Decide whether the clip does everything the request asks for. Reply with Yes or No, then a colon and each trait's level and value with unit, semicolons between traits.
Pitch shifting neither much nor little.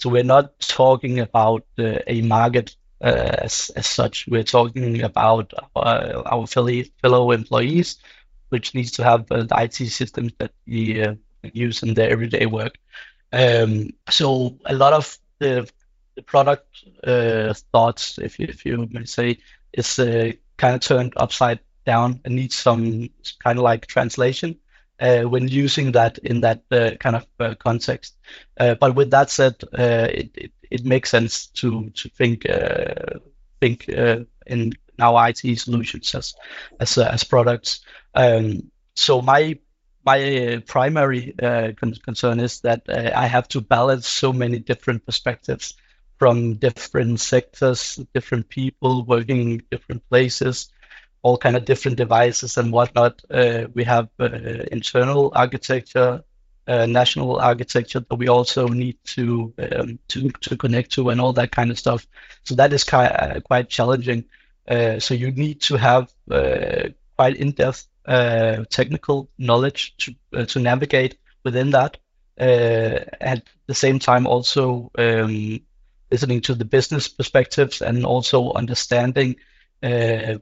No: narrow, 1.9 semitones